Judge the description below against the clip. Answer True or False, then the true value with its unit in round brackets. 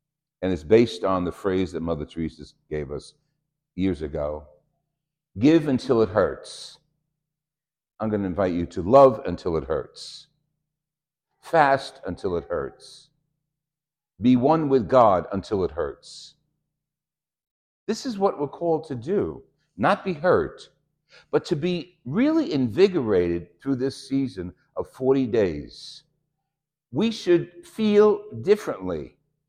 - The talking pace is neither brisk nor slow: False (125 wpm)